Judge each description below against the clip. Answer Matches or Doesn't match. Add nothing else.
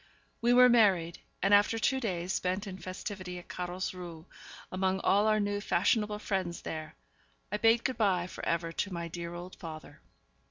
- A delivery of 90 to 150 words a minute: Doesn't match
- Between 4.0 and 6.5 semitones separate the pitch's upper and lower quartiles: Doesn't match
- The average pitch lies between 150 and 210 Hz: Matches